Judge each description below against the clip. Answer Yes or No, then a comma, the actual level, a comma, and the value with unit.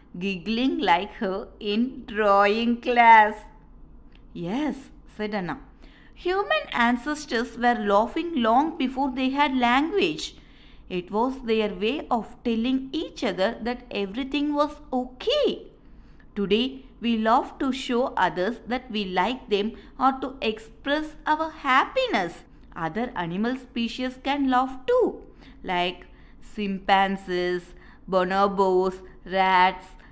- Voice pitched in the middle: No, high, 240 Hz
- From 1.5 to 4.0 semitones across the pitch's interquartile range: No, average, 5.0 semitones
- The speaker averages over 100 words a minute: Yes, average, 110 wpm